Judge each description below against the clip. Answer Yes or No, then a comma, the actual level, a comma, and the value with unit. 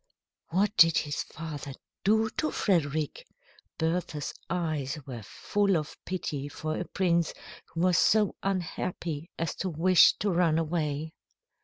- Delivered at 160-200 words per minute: No, slow, 135 wpm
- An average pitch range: Yes, average, 3.2 semitones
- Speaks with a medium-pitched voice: Yes, medium, 165 Hz